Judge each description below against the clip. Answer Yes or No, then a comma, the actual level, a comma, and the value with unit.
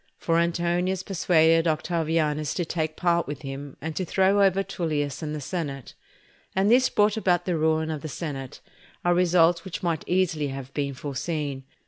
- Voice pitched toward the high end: No, medium, 165 Hz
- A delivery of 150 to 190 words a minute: Yes, average, 170 wpm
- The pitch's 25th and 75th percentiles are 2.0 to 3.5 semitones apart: Yes, average, 3.1 semitones